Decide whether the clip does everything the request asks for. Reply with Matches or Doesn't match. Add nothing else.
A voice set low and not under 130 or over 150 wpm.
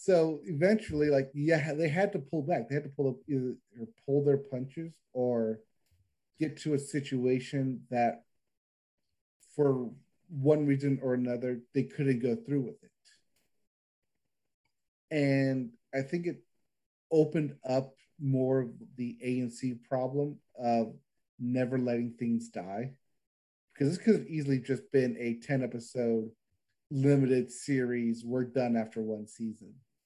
Matches